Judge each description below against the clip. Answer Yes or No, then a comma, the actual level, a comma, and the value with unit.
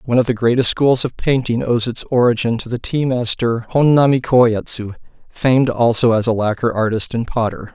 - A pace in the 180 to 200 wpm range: Yes, average, 185 wpm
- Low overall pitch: Yes, low, 120 Hz